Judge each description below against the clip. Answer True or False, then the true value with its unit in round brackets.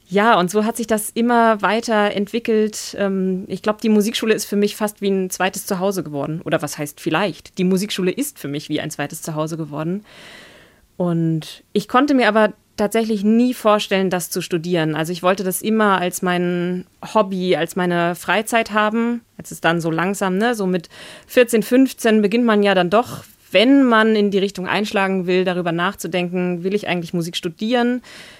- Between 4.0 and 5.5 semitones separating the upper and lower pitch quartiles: False (3.5 semitones)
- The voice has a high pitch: True (195 Hz)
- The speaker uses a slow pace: False (185 wpm)